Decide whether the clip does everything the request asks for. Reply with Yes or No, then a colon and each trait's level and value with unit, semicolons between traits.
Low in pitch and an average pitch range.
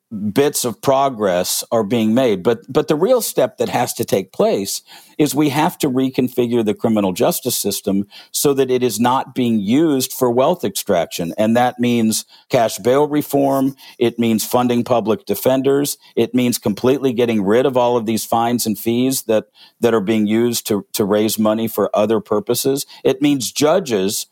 Yes: low, 120 Hz; average, 3.5 semitones